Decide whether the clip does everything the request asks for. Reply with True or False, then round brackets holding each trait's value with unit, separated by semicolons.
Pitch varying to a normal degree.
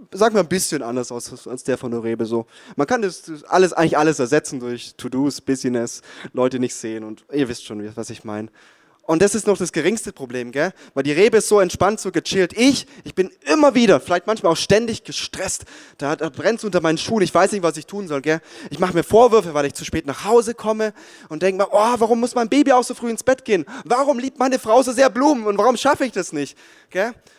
False (8.4 semitones)